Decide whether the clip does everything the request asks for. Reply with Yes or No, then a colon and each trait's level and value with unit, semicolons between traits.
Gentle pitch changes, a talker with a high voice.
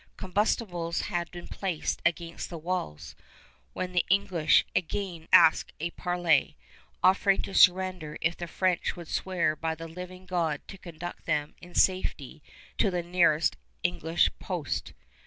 No: narrow, 2.2 semitones; medium, 175 Hz